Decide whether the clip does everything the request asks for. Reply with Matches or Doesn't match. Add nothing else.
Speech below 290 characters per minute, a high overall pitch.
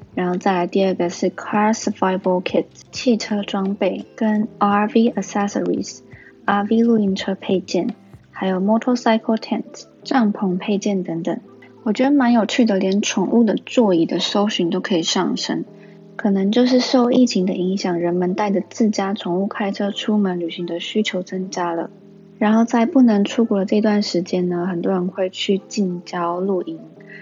Doesn't match